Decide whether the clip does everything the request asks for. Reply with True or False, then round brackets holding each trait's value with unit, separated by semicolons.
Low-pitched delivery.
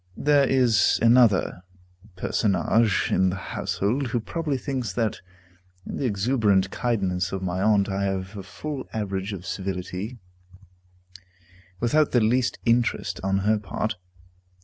True (105 Hz)